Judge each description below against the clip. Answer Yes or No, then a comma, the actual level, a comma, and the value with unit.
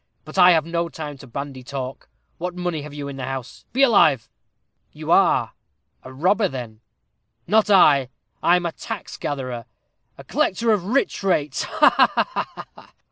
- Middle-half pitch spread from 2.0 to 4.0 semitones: No, average, 5.3 semitones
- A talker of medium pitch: Yes, medium, 155 Hz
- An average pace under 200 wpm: Yes, average, 160 wpm